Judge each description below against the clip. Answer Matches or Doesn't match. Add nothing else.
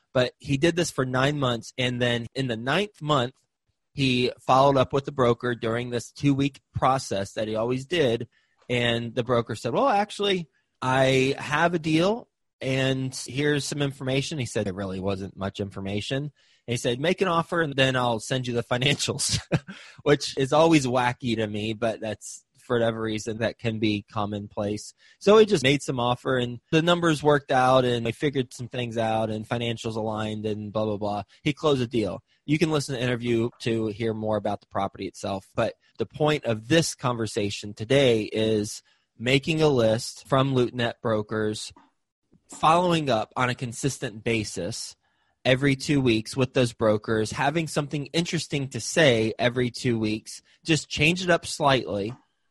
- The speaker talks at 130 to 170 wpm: Doesn't match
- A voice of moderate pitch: Doesn't match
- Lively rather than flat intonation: Doesn't match